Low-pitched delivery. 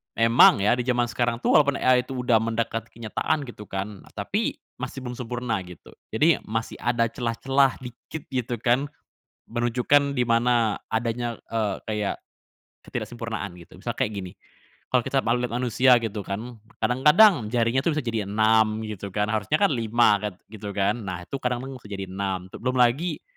Yes: low, 115 Hz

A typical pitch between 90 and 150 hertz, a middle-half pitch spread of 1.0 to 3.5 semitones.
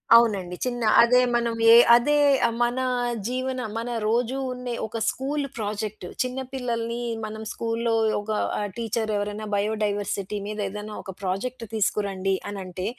No: high, 220 Hz; average, 2.8 semitones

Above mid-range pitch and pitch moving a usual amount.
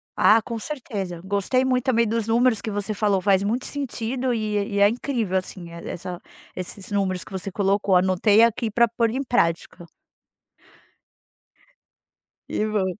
Yes: high, 210 Hz; average, 3.5 semitones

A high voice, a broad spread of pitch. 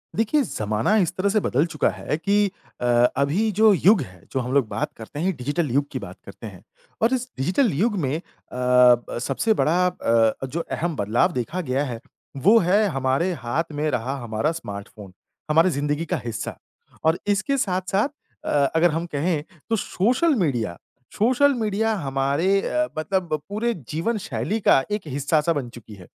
No: medium, 155 Hz; wide, 7.7 semitones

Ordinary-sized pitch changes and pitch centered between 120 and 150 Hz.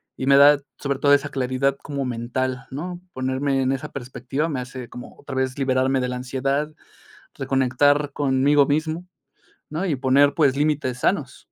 No: narrow, 1.8 semitones; low, 135 Hz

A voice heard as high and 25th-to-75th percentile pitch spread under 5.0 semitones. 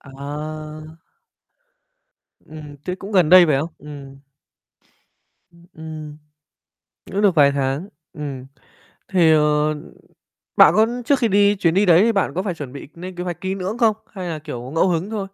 No: medium, 165 Hz; average, 4.1 semitones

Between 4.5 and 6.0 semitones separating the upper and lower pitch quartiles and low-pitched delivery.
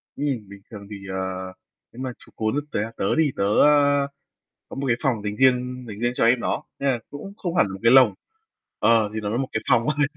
Yes: average, 4.8 semitones; low, 120 Hz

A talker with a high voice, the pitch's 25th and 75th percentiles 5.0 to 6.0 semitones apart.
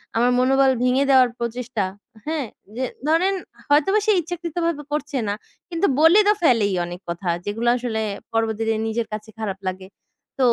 Yes: very high, 250 Hz; wide, 5.6 semitones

